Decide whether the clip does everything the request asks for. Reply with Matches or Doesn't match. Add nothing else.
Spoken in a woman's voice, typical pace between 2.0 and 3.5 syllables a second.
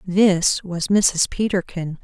Matches